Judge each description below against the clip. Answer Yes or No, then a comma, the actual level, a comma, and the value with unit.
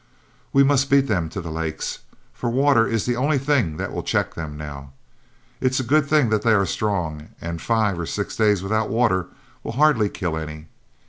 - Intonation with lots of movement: Yes, wide, 7.7 semitones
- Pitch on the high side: No, low, 110 Hz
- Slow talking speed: No, average, 200 wpm